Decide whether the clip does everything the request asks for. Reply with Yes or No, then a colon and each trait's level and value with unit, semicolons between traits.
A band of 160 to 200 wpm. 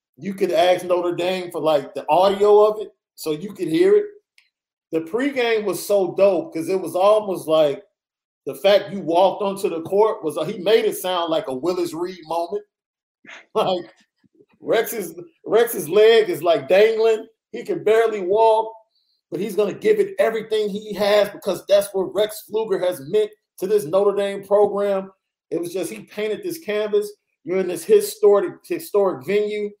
Yes: average, 175 wpm